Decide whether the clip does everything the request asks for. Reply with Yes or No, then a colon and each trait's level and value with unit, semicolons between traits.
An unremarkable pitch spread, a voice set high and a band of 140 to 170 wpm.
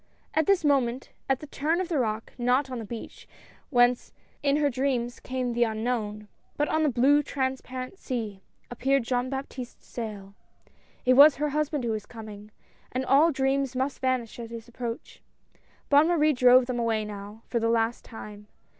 No: average, 3.3 semitones; very high, 250 Hz; average, 185 wpm